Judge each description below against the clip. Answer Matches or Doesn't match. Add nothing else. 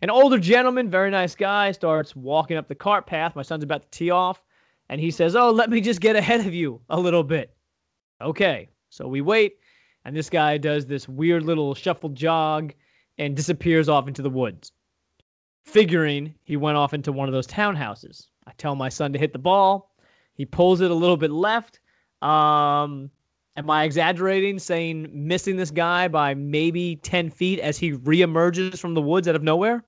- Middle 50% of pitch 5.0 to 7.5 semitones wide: Doesn't match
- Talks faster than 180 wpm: Matches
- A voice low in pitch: Doesn't match